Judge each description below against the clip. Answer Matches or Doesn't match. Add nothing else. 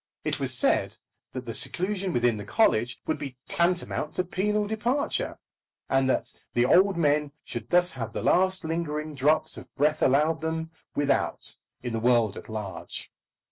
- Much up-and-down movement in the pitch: Matches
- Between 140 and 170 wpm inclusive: Matches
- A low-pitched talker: Doesn't match